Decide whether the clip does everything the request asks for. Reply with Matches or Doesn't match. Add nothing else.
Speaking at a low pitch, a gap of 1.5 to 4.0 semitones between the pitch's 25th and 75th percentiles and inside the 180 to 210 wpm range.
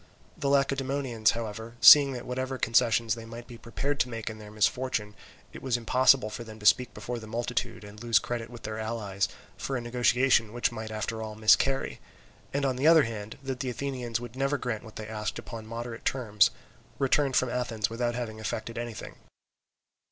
Matches